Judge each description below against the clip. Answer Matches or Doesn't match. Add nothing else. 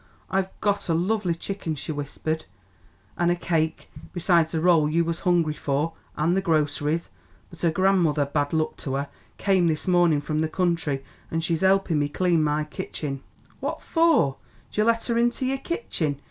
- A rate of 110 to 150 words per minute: Doesn't match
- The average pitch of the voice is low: Doesn't match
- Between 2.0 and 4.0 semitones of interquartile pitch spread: Matches